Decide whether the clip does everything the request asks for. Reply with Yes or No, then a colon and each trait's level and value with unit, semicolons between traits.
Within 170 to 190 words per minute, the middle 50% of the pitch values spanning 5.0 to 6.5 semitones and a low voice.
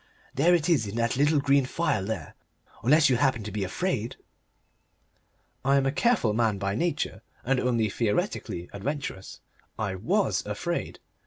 No: average, 155 wpm; average, 5.3 semitones; low, 125 Hz